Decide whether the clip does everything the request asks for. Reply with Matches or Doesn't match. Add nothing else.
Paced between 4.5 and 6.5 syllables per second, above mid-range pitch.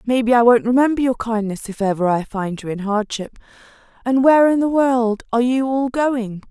Matches